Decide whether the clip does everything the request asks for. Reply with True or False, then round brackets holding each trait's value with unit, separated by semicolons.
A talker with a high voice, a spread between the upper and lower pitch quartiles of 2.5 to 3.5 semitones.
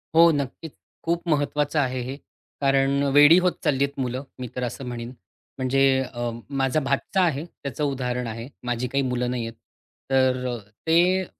False (135 Hz; 2.8 semitones)